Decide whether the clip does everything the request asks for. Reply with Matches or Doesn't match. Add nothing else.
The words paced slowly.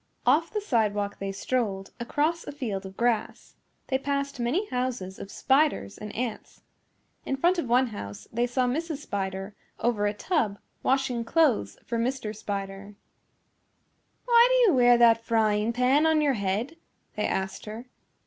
Doesn't match